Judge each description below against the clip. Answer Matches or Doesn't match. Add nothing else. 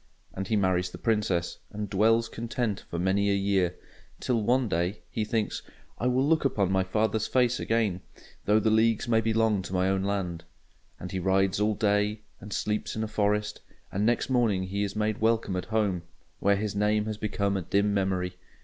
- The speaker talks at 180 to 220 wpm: Matches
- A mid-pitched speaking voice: Doesn't match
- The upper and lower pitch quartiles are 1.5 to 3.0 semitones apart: Matches